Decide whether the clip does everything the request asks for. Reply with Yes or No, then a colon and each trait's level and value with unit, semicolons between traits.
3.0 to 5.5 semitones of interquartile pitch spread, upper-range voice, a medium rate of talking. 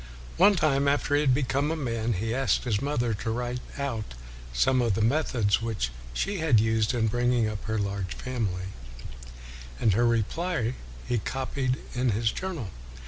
No: average, 3.8 semitones; low, 120 Hz; average, 175 wpm